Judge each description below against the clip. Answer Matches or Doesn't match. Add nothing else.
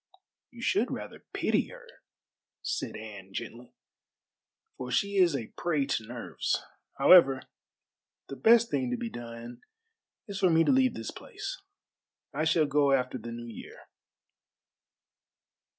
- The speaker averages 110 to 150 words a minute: Matches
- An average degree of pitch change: Doesn't match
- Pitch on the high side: Doesn't match